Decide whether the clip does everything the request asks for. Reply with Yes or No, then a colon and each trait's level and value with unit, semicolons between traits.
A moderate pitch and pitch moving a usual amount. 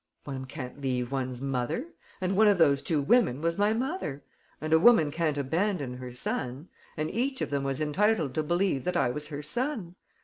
No: medium, 155 Hz; wide, 6.4 semitones